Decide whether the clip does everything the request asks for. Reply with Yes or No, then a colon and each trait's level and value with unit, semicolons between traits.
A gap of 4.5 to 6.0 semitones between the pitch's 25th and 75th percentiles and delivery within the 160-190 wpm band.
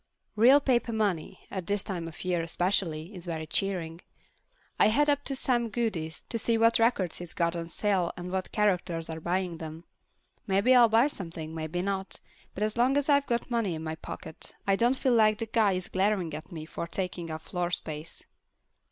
No: average, 5.3 semitones; average, 200 wpm